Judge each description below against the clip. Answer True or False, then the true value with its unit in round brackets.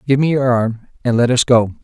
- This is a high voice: False (125 Hz)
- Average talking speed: False (260 wpm)